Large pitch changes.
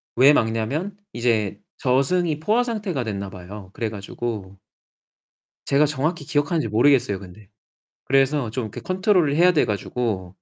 Yes: wide, 6.5 semitones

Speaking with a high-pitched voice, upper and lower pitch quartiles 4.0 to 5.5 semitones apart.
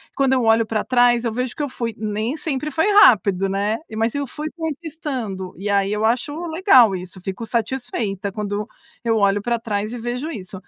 Yes: high, 230 Hz; average, 4.4 semitones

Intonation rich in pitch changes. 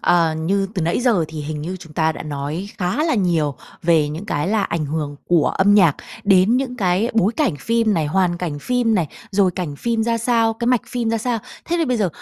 Yes: wide, 6.2 semitones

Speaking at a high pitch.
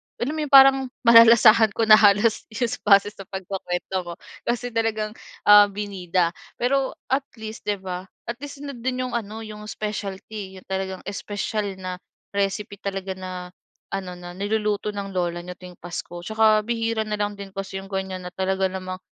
Yes: high, 205 Hz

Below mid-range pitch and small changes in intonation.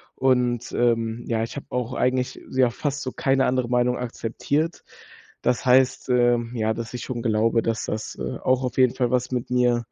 Yes: low, 125 Hz; narrow, 1.6 semitones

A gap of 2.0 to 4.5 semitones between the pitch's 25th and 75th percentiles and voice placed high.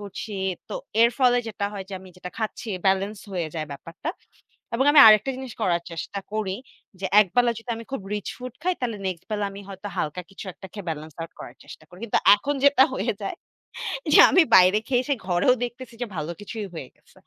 No: average, 4.9 semitones; high, 205 Hz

